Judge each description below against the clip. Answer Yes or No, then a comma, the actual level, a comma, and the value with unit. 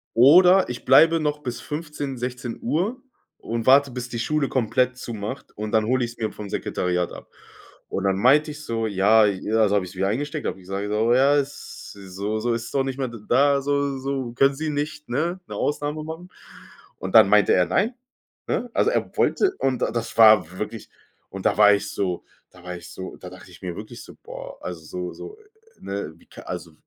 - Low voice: Yes, low, 120 Hz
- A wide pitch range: Yes, wide, 5.9 semitones